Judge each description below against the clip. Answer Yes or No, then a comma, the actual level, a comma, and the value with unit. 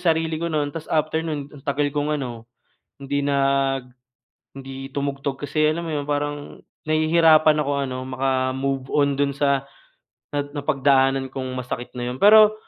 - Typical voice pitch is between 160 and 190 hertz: No, medium, 140 Hz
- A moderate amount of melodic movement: No, narrow, 2.3 semitones